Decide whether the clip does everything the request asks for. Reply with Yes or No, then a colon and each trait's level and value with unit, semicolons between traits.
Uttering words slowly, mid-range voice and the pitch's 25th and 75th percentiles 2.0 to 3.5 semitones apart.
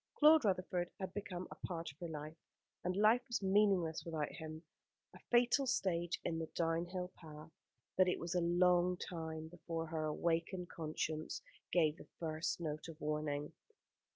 No: average, 160 wpm; medium, 170 Hz; narrow, 2.5 semitones